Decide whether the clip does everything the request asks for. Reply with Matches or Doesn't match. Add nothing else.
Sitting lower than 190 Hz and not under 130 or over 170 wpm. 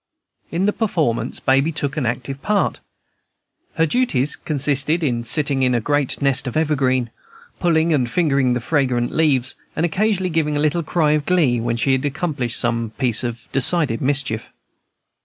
Matches